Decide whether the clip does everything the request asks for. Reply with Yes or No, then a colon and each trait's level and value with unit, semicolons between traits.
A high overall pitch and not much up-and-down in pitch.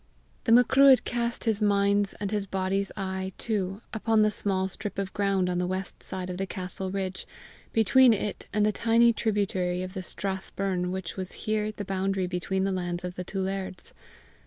Yes: high, 195 Hz; narrow, 2.1 semitones